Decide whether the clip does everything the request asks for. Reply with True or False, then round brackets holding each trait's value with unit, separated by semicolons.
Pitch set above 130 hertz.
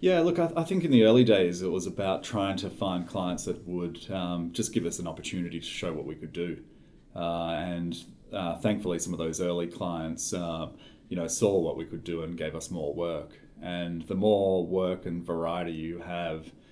False (85 Hz)